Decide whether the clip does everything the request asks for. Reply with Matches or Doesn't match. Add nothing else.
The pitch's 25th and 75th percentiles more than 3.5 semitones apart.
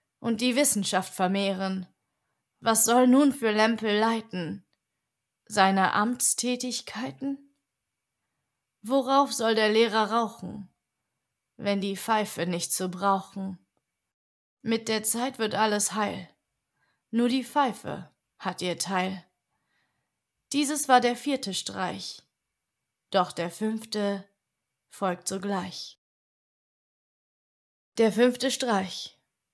Matches